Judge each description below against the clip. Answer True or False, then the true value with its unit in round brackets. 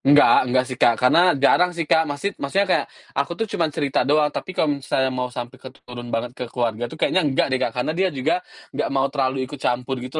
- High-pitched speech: False (135 Hz)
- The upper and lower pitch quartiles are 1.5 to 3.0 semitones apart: False (3.8 semitones)